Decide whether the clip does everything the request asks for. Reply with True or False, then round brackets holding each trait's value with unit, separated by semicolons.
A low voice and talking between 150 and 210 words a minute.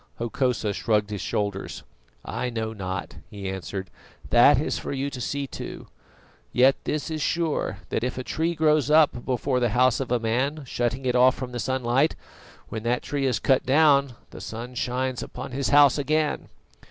True (125 Hz; 180 wpm)